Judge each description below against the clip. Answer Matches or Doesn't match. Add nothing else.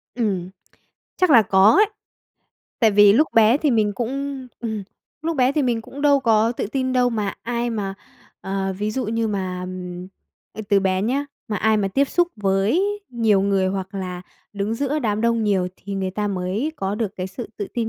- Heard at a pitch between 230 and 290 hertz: Doesn't match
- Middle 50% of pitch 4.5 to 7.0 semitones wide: Doesn't match